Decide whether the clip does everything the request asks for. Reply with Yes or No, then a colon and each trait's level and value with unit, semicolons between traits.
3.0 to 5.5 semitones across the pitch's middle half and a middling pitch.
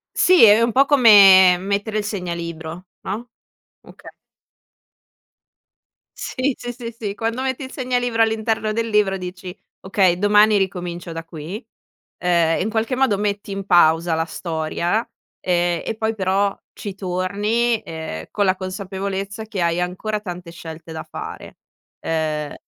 No: average, 3.9 semitones; high, 195 Hz